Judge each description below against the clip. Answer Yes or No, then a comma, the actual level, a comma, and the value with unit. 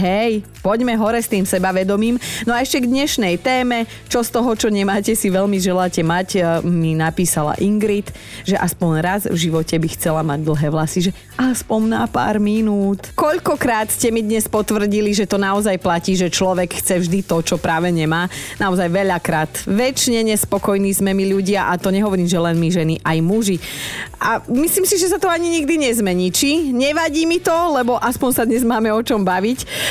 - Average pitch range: Yes, average, 4.6 semitones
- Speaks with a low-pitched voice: No, high, 200 Hz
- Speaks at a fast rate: Yes, fast, 185 wpm